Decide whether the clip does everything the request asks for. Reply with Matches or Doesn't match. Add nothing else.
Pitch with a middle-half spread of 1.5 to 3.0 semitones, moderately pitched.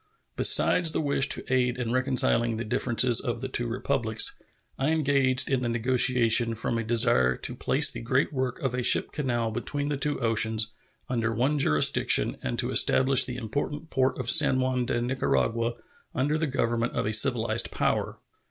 Doesn't match